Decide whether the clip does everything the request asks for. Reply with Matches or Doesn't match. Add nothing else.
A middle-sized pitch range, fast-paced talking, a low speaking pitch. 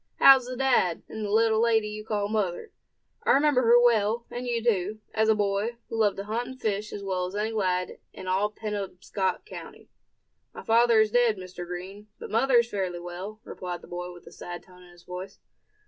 Doesn't match